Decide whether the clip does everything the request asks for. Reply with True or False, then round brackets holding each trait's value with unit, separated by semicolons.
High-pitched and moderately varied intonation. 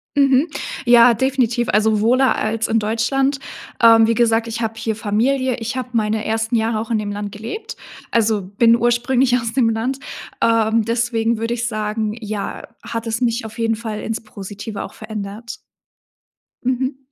False (225 Hz; 1.7 semitones)